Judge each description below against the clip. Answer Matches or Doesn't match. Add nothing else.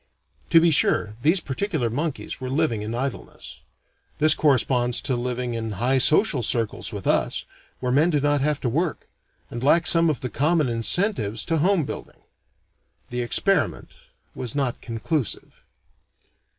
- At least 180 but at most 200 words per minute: Doesn't match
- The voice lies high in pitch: Doesn't match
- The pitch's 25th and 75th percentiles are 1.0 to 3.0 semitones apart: Doesn't match